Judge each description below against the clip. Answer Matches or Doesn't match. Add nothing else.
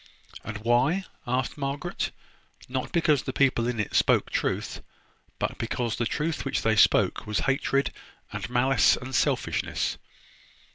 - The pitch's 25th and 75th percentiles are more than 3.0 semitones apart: Doesn't match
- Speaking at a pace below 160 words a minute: Matches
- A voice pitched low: Matches